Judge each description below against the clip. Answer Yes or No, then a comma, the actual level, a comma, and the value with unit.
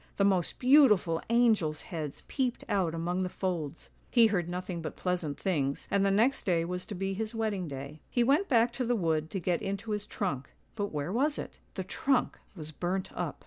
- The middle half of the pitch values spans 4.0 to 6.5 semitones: Yes, average, 5.1 semitones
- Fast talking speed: Yes, fast, 215 wpm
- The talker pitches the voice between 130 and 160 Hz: No, medium, 185 Hz